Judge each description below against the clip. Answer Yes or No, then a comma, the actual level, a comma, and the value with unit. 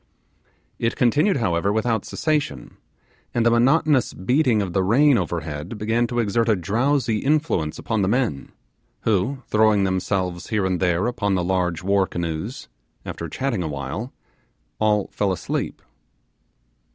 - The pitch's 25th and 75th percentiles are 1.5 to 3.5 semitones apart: No, average, 4.8 semitones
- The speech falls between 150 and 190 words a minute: No, average, 140 wpm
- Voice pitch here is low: Yes, low, 105 Hz